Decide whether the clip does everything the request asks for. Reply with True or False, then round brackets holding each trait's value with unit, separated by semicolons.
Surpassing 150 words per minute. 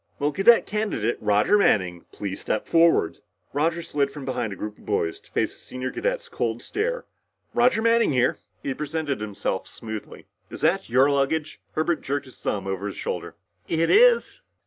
True (175 wpm)